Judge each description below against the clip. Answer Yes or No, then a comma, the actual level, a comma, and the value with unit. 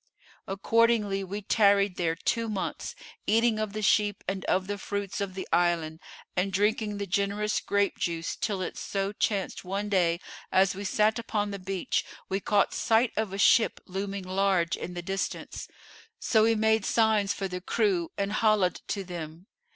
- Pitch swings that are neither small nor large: No, narrow, 2.1 semitones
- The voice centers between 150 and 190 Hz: No, high, 200 Hz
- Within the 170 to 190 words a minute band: Yes, average, 175 wpm